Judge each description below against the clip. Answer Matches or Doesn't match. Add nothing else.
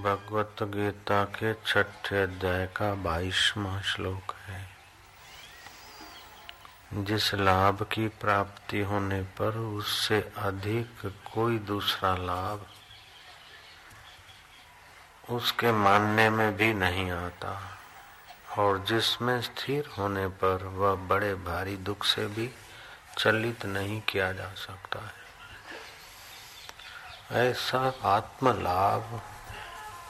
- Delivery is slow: Matches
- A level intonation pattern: Matches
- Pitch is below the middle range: Matches